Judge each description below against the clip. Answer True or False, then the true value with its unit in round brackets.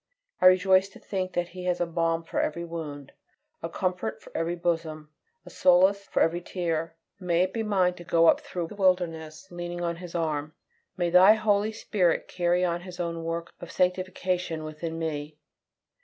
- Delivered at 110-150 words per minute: False (185 wpm)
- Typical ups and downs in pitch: False (1.9 semitones)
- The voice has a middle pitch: True (175 Hz)